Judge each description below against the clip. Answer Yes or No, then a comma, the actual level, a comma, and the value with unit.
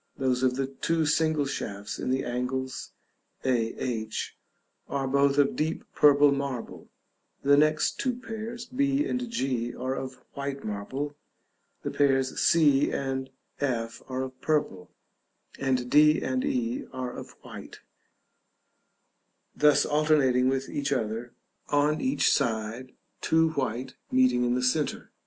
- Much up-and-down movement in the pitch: No, average, 2.8 semitones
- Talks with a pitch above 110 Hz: Yes, low, 135 Hz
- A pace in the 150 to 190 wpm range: No, slow, 135 wpm